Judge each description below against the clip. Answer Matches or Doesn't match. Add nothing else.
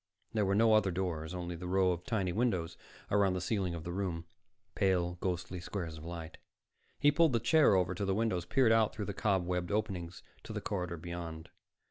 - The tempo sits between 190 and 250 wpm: Matches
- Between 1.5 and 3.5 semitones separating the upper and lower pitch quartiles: Matches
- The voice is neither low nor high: Doesn't match